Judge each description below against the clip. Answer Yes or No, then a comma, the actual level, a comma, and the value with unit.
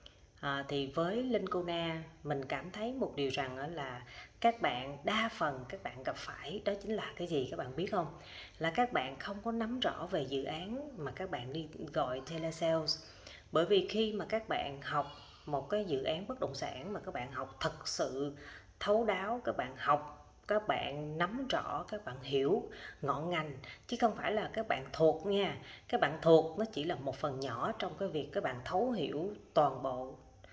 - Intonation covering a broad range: Yes, wide, 6.8 semitones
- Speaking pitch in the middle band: Yes, medium, 160 Hz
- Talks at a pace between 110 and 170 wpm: No, average, 210 wpm